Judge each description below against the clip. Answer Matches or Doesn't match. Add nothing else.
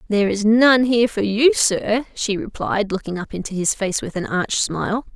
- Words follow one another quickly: Matches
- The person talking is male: Doesn't match